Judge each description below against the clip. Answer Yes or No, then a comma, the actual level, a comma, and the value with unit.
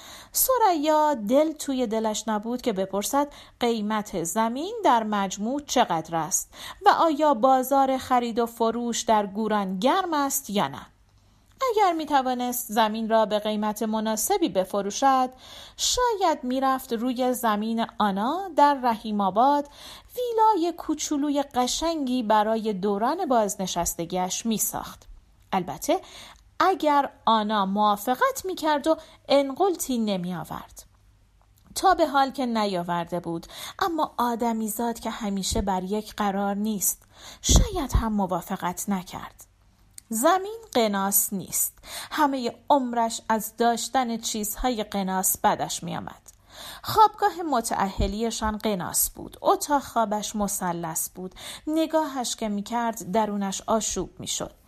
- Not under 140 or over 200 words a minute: No, average, 115 wpm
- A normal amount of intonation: No, wide, 5.9 semitones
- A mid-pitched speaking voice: No, high, 230 Hz